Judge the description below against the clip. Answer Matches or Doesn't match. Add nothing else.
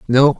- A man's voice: Matches